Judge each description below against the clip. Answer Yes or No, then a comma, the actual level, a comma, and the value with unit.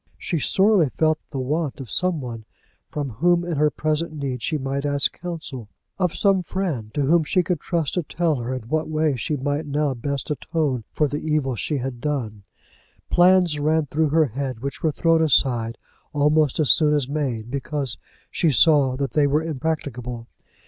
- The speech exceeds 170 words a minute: Yes, average, 185 wpm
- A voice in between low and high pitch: Yes, medium, 145 Hz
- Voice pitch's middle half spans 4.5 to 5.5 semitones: No, average, 3.3 semitones